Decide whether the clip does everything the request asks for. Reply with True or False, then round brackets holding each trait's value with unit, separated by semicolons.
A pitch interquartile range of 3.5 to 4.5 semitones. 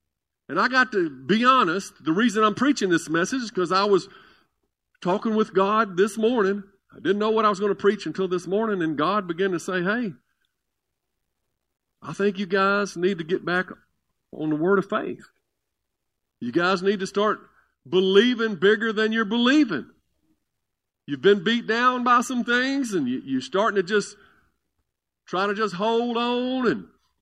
False (3.1 semitones)